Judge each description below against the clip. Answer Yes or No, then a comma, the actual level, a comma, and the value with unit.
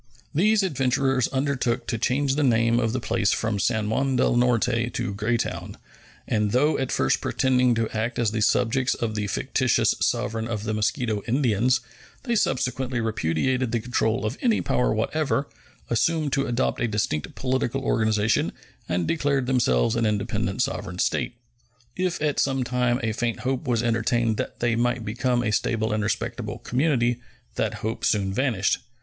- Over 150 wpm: Yes, average, 165 wpm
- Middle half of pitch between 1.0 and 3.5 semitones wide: Yes, average, 3.2 semitones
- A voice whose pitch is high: No, low, 120 Hz